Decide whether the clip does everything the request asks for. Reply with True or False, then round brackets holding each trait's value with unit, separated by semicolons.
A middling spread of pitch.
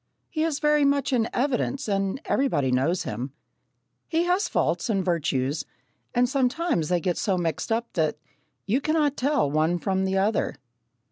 False (8.7 semitones)